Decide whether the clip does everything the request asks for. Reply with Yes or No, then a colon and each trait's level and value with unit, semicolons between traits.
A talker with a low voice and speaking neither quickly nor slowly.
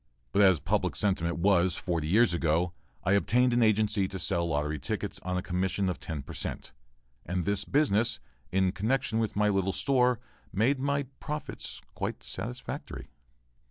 Yes: very low, 95 Hz; average, 160 wpm